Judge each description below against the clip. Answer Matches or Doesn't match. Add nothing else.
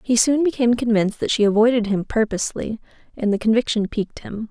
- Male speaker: Doesn't match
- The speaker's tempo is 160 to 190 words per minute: Matches